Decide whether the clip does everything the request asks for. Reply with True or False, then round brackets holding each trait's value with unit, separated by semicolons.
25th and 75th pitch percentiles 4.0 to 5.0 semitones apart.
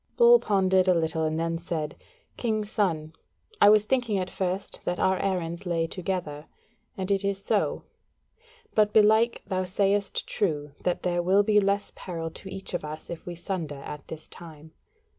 False (3.5 semitones)